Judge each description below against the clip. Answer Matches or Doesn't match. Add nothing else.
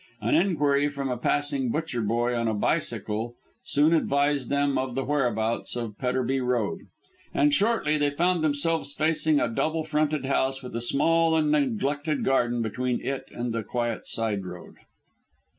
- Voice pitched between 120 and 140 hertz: Matches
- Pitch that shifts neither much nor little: Matches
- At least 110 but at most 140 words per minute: Doesn't match